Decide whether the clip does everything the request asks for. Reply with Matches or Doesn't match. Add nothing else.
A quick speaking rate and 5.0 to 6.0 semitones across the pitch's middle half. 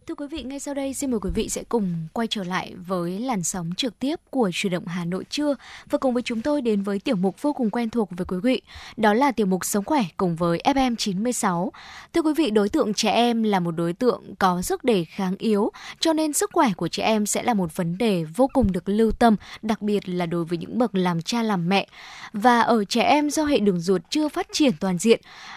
Matches